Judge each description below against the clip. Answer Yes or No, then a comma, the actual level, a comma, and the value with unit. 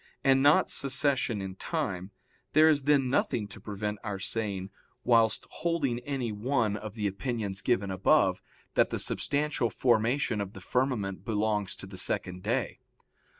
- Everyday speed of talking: Yes, average, 160 wpm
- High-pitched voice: No, low, 110 Hz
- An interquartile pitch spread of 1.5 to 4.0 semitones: No, average, 4.9 semitones